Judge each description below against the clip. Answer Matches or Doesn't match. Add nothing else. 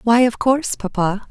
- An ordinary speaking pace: Matches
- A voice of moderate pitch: Doesn't match